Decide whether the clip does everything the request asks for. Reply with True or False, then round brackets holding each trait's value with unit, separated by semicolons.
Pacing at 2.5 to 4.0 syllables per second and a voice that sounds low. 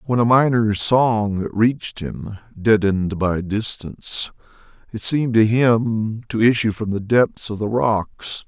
True (3.9 syllables/s; 110 Hz)